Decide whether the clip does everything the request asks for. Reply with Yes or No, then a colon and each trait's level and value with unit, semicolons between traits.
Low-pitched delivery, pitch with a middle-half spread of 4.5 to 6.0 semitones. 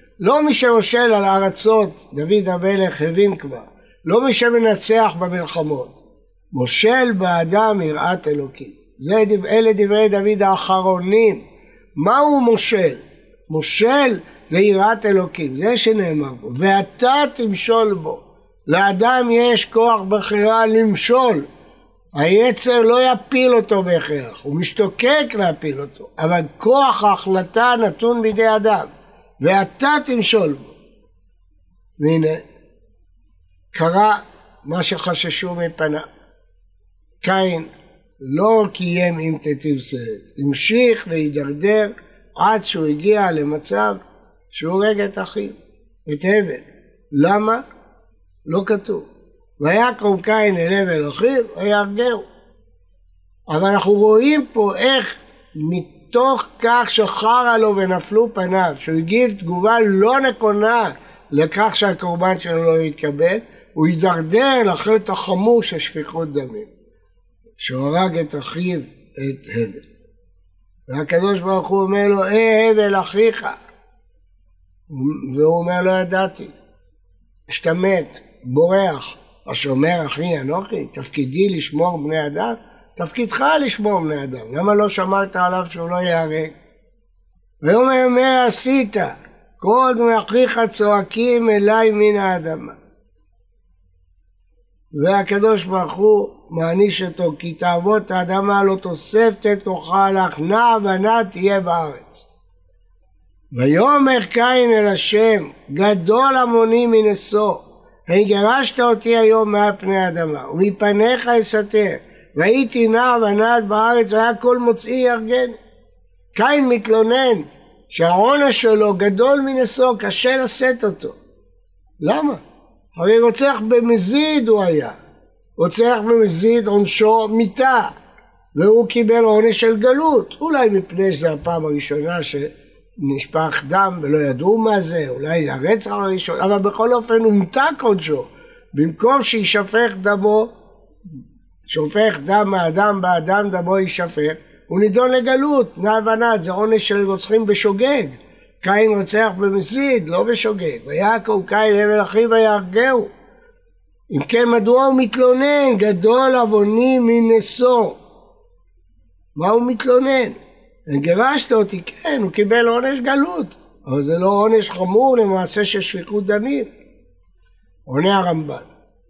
No: high, 205 Hz; wide, 5.6 semitones